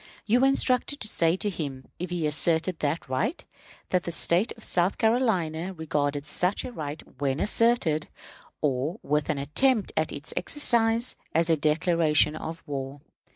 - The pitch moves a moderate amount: No, wide, 6.1 semitones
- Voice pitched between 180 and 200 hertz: No, medium, 165 Hz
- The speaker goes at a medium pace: Yes, average, 160 wpm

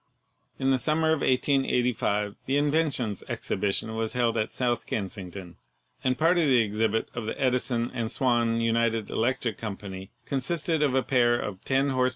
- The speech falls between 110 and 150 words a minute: No, average, 175 wpm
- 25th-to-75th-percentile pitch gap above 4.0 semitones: No, average, 3.3 semitones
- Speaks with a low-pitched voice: Yes, low, 120 Hz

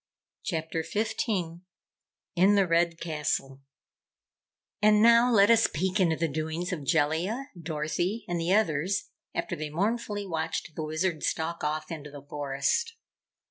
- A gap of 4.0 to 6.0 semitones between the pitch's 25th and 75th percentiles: Yes, average, 4.5 semitones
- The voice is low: No, medium, 170 Hz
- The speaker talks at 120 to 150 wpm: Yes, average, 140 wpm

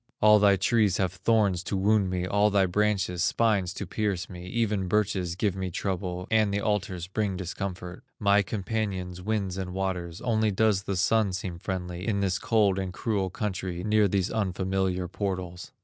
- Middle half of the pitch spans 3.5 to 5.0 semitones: No, narrow, 2.4 semitones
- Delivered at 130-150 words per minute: No, average, 175 wpm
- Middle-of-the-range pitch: No, very low, 95 Hz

